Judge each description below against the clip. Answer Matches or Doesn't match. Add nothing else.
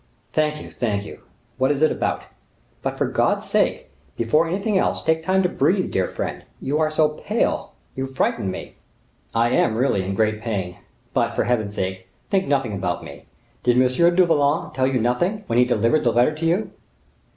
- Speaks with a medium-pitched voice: Doesn't match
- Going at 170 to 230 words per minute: Matches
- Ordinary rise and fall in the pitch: Doesn't match